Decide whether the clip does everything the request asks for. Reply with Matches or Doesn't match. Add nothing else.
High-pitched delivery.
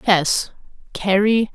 Matches